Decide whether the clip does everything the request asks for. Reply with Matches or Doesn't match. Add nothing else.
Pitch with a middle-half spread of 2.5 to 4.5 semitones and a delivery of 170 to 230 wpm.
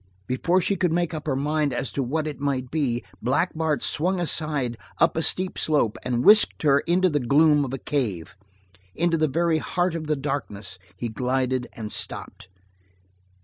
Matches